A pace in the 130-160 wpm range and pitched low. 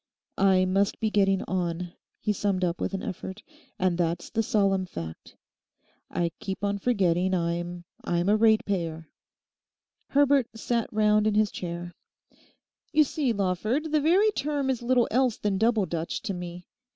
No: average, 150 wpm; high, 195 Hz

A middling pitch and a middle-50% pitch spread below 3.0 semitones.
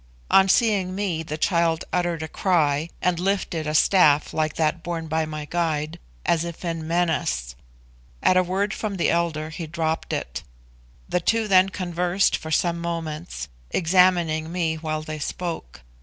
Yes: medium, 170 Hz; narrow, 2.5 semitones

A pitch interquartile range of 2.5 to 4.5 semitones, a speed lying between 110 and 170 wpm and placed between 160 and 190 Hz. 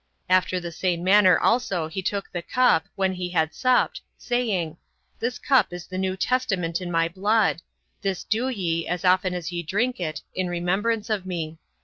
No: average, 3.2 semitones; average, 180 wpm; medium, 185 Hz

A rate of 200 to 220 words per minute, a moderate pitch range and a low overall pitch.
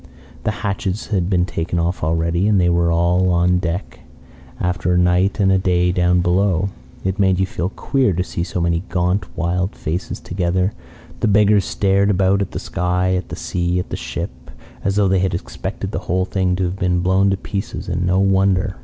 No: fast, 205 wpm; narrow, 1.6 semitones; very low, 90 Hz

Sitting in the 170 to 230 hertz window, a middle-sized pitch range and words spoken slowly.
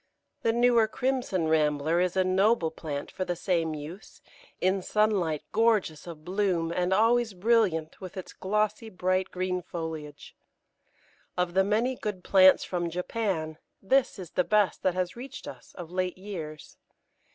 No: medium, 185 Hz; average, 4.1 semitones; average, 150 wpm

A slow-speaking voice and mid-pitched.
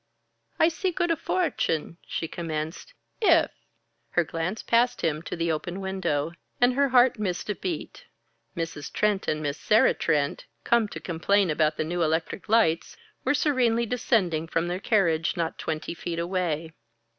No: average, 165 wpm; medium, 175 Hz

